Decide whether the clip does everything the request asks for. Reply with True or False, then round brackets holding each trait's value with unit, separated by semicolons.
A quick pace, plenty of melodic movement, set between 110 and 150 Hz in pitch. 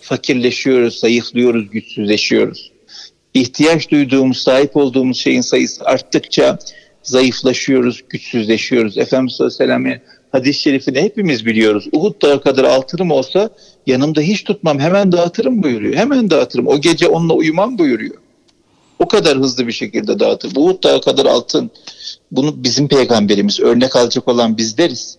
False (130 wpm; 5.8 semitones; 135 Hz)